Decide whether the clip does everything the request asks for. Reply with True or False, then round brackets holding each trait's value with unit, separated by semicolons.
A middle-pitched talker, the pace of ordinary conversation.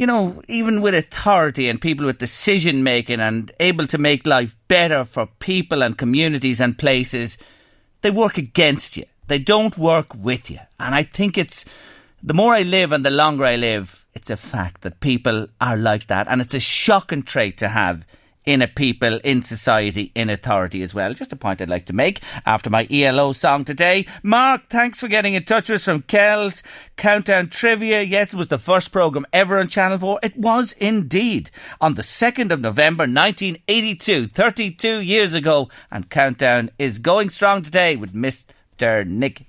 True (155 Hz; 185 wpm)